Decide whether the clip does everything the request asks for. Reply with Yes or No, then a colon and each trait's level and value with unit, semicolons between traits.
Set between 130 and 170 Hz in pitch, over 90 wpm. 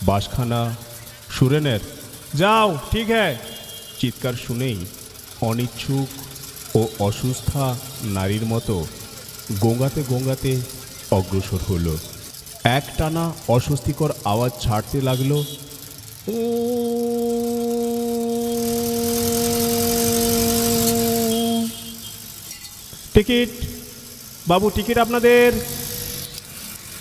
No: low, 135 Hz; average, 60 wpm